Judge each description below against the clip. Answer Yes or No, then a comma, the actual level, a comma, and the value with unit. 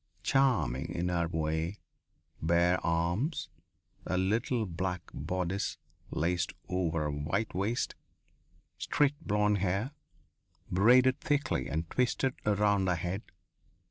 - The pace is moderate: No, slow, 110 wpm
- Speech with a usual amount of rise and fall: Yes, average, 4.2 semitones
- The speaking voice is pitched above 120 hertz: No, very low, 95 Hz